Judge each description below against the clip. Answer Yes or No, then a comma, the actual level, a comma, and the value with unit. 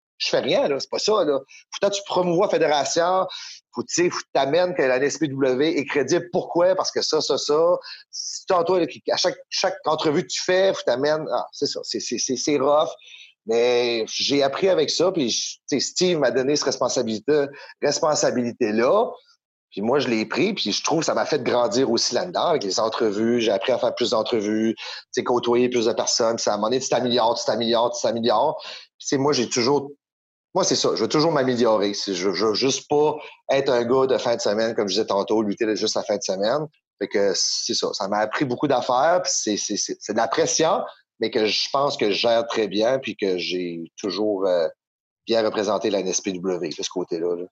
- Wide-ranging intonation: Yes, wide, 8.2 semitones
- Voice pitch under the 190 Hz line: Yes, medium, 140 Hz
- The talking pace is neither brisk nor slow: No, fast, 220 wpm